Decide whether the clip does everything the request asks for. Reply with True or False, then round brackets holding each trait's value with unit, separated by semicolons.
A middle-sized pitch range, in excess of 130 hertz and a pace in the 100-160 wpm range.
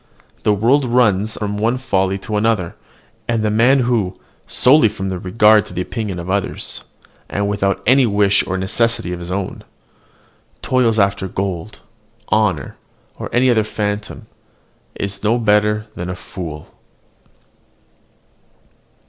False (3.1 semitones; 105 Hz; 140 wpm)